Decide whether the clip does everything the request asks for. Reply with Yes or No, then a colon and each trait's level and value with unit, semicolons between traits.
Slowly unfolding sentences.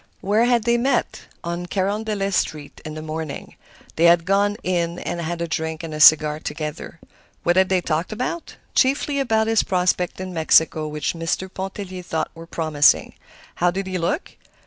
No: average, 175 wpm